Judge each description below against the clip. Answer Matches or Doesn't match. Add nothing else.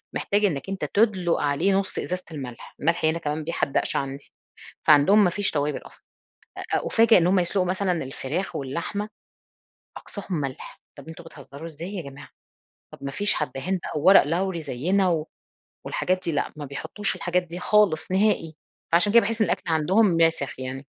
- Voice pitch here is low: Doesn't match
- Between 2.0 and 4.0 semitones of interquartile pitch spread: Doesn't match